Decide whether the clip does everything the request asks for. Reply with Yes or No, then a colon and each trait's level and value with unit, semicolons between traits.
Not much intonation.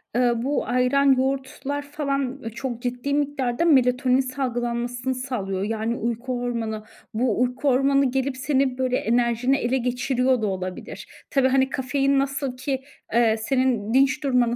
Yes: narrow, 2.1 semitones